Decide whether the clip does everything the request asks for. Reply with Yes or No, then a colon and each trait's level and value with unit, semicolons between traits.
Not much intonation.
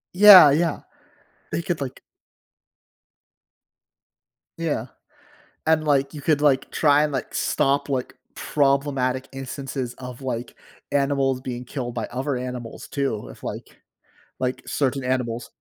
Yes: narrow, 2.3 semitones